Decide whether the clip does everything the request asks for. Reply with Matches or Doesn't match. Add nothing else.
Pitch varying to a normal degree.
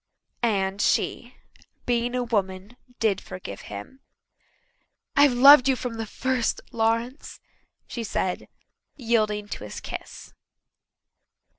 Matches